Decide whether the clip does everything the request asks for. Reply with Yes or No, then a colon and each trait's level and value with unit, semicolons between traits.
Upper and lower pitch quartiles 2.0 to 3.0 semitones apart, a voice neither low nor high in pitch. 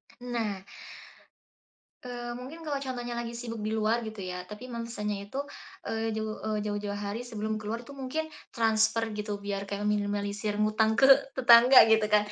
No: narrow, 2.4 semitones; high, 220 Hz